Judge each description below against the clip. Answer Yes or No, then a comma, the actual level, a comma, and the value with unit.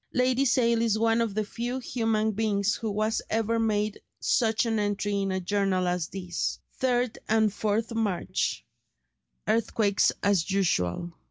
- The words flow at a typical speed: Yes, average, 155 wpm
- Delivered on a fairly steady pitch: Yes, narrow, 2.3 semitones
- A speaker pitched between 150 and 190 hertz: No, high, 215 Hz